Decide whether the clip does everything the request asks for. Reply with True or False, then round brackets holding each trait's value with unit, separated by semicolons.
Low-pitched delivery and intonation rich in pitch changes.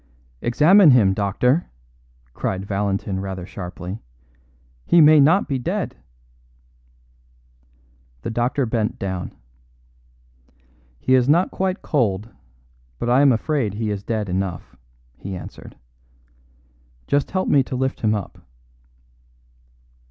True (115 Hz; 6.2 semitones)